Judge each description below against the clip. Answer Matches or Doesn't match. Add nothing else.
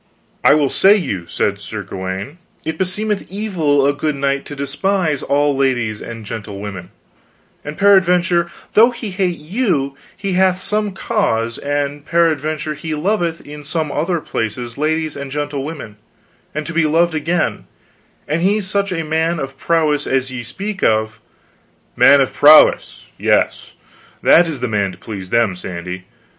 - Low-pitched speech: Doesn't match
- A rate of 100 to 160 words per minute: Matches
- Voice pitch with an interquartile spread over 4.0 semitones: Matches